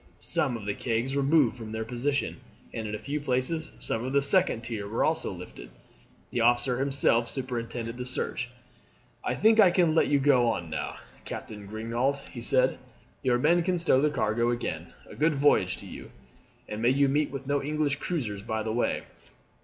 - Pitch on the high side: No, low, 125 Hz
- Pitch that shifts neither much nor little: Yes, average, 4.0 semitones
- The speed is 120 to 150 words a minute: No, average, 195 wpm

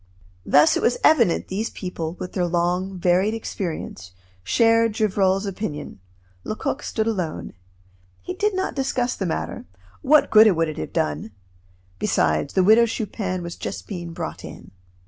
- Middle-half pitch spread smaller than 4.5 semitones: No, average, 4.8 semitones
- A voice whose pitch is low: No, high, 190 Hz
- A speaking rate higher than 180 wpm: No, average, 150 wpm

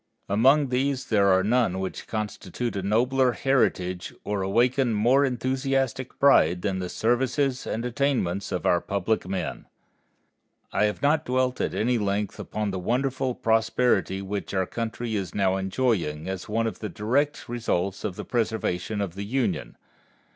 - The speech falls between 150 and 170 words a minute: Yes, average, 155 wpm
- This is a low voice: Yes, low, 110 Hz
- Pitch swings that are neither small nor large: Yes, average, 4.7 semitones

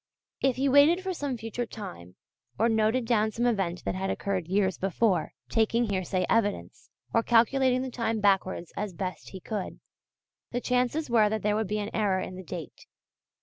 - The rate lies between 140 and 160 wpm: No, average, 185 wpm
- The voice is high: Yes, high, 215 Hz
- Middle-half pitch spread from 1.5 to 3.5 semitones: No, average, 4.0 semitones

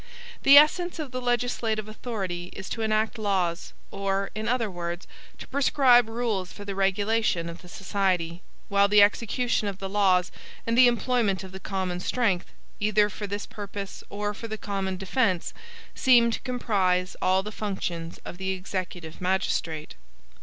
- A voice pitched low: No, high, 200 Hz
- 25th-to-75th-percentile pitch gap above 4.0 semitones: No, average, 3.4 semitones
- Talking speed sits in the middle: Yes, average, 160 wpm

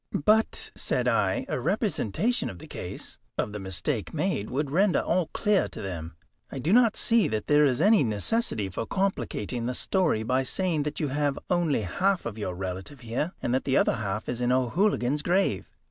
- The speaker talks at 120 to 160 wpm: No, average, 190 wpm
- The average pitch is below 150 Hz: Yes, low, 135 Hz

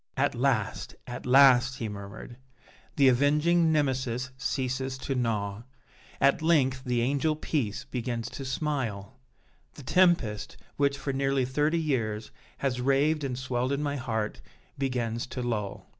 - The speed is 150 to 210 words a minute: No, average, 140 wpm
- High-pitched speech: No, low, 130 Hz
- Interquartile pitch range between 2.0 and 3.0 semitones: Yes, average, 2.7 semitones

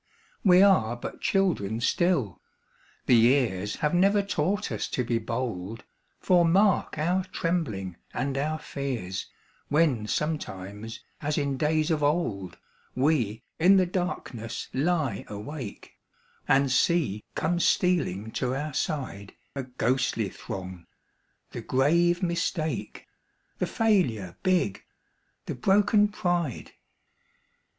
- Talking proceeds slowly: Yes, slow, 115 wpm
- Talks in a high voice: No, medium, 140 Hz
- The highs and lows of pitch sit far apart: Yes, wide, 7.7 semitones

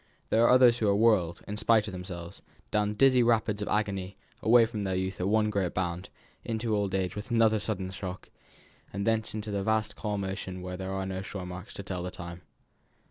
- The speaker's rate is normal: No, fast, 215 wpm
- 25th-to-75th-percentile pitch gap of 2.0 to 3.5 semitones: Yes, average, 2.7 semitones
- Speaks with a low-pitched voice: Yes, low, 100 Hz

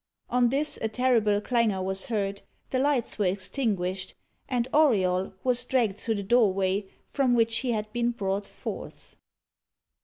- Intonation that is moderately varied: Yes, average, 4.0 semitones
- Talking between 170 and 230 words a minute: No, average, 150 wpm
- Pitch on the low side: No, high, 220 Hz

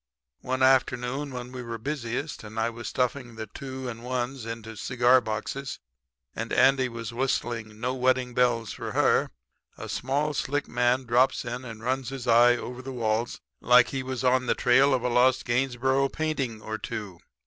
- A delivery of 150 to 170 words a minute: No, average, 180 wpm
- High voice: No, low, 125 Hz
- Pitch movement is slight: Yes, narrow, 2.0 semitones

